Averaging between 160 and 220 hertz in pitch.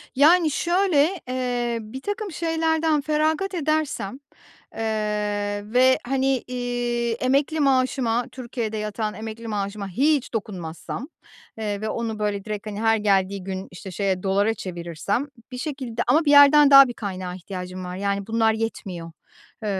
No: high, 235 Hz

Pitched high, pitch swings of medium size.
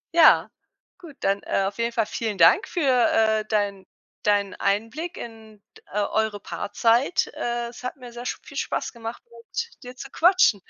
Yes: high, 230 Hz; average, 3.4 semitones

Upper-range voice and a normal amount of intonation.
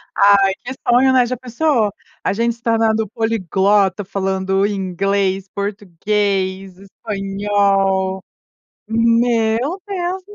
Yes: high, 205 Hz; average, 3.1 semitones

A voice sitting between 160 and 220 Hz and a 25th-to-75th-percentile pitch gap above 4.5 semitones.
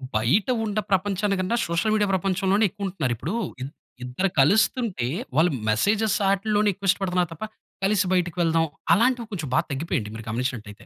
Yes: medium, 185 Hz; average, 5.0 semitones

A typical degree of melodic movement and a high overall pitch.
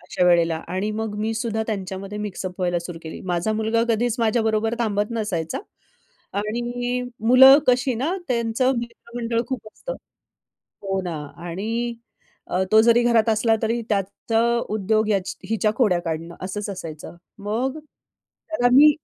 Yes: average, 3.6 semitones; high, 220 Hz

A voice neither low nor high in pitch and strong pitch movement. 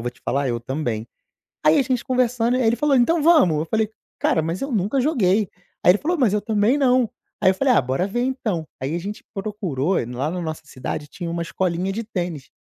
No: high, 195 Hz; wide, 7.6 semitones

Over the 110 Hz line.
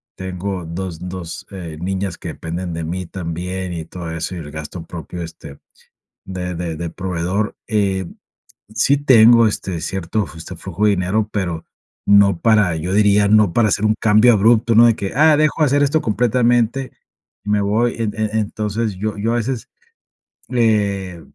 No: low, 100 Hz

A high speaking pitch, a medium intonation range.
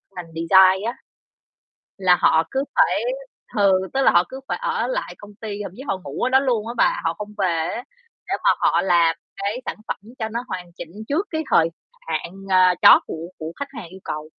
No: high, 195 Hz; wide, 5.8 semitones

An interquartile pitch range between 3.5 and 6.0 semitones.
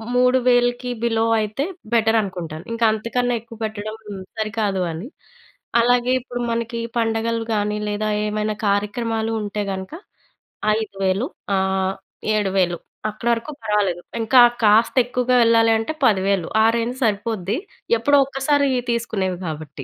No: average, 2.9 semitones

